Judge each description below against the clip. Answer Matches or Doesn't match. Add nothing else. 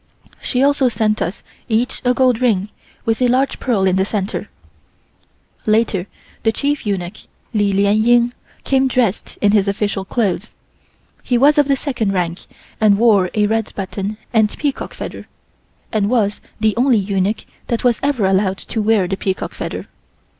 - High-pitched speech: Matches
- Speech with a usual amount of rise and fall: Matches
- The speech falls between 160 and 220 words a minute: Matches